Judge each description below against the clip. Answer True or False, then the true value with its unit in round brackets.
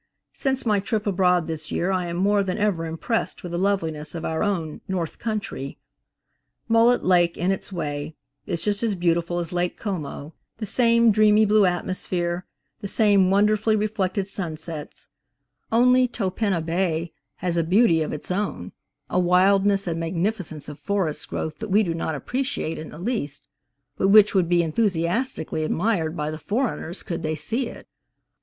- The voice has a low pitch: False (185 Hz)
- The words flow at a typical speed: True (165 wpm)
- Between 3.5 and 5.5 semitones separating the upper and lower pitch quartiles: True (4.1 semitones)